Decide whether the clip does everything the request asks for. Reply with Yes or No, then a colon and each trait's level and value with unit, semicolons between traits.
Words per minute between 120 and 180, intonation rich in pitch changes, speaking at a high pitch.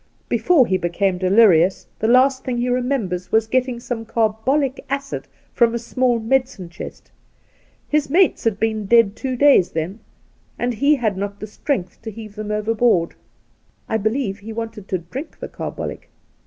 No: average, 165 wpm; average, 4.0 semitones; high, 225 Hz